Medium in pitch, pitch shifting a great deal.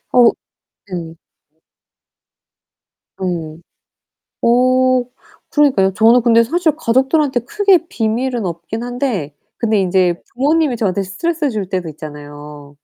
No: high, 230 Hz; wide, 6.4 semitones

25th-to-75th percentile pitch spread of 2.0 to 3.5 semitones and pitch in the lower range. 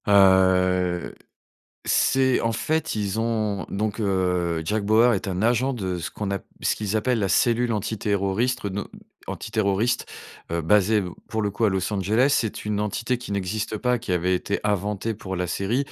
Yes: average, 3.1 semitones; low, 105 Hz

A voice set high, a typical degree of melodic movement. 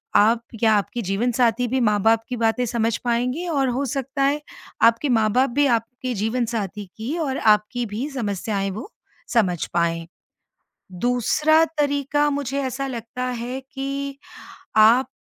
Yes: high, 245 Hz; average, 3.7 semitones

